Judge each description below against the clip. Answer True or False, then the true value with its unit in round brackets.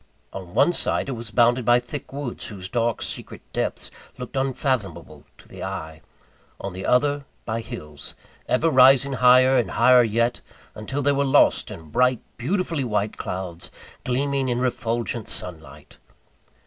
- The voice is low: True (120 Hz)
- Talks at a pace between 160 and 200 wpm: False (150 wpm)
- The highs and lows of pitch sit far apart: False (4.2 semitones)